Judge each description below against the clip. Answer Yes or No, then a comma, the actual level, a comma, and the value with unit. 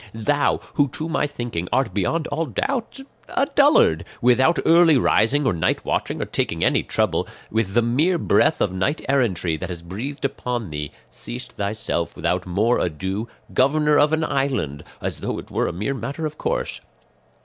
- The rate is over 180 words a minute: No, average, 175 wpm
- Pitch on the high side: No, low, 125 Hz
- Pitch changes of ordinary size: No, wide, 8.0 semitones